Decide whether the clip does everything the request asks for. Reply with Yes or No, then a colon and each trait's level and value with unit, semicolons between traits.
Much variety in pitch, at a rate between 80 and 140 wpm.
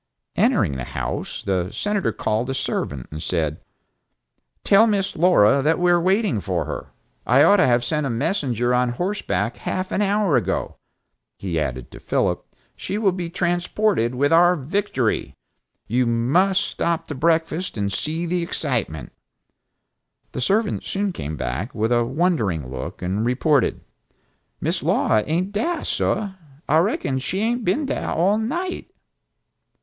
No: wide, 8.8 semitones; average, 155 wpm